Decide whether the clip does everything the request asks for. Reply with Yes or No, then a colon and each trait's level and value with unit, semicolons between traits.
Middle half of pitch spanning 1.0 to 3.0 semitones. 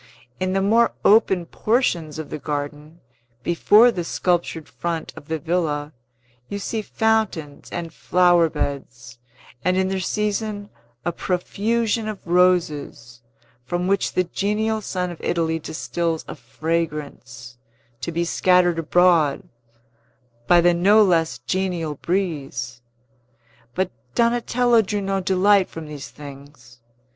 No: average, 4.4 semitones